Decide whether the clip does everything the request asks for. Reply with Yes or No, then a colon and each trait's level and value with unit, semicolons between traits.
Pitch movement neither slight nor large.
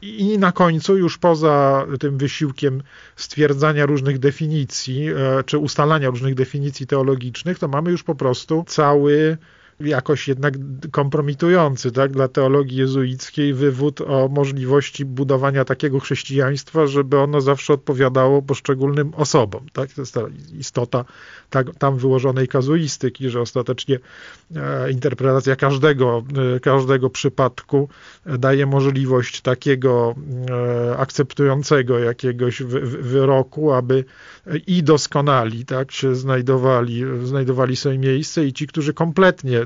No: narrow, 1.9 semitones